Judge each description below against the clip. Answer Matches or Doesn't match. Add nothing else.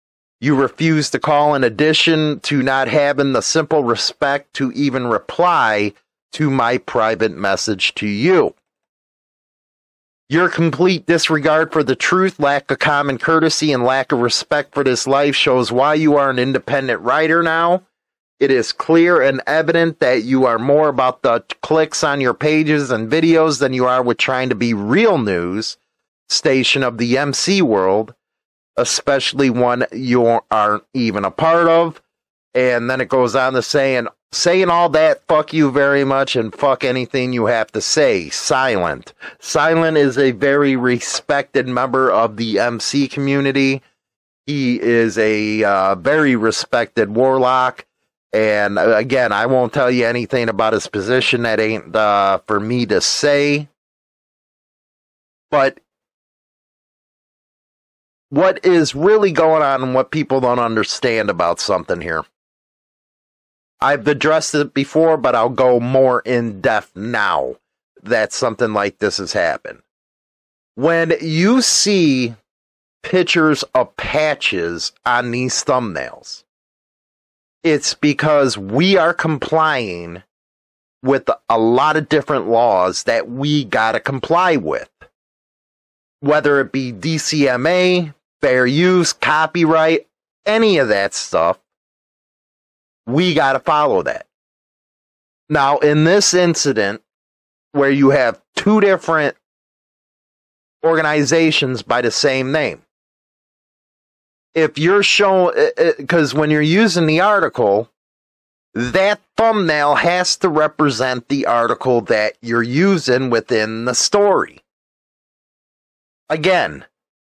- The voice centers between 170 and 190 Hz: Doesn't match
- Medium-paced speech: Doesn't match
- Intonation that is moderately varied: Matches